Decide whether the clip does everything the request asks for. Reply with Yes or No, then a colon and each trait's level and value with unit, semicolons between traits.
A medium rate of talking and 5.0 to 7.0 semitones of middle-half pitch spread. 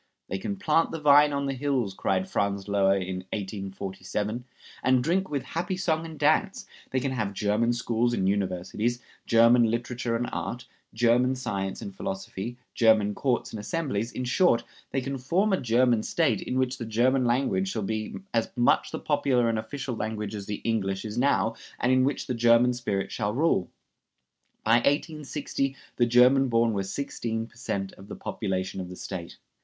No: average, 180 wpm; average, 4.3 semitones